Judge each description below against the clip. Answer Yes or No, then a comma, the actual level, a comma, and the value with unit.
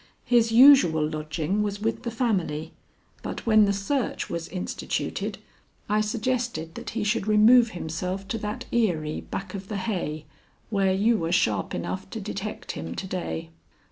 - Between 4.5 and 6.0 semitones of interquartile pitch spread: Yes, wide, 5.4 semitones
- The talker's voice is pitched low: No, high, 200 Hz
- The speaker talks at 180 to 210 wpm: No, average, 160 wpm